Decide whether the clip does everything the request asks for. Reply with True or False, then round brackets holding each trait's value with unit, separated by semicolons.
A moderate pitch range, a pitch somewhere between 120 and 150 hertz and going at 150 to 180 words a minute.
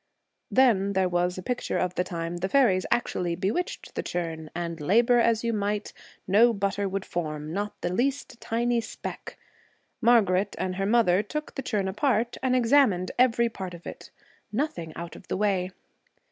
False (4.7 semitones; 200 Hz; 175 wpm)